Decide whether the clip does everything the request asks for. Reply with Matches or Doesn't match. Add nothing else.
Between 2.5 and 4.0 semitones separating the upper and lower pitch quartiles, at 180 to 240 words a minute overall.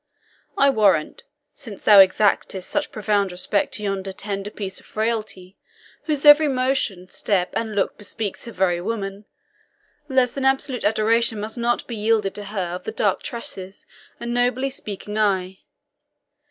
Doesn't match